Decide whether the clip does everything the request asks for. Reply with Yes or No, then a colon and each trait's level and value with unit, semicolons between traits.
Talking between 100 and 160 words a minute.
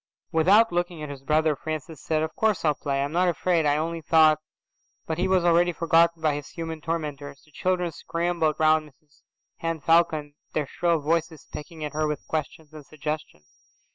No: average, 190 wpm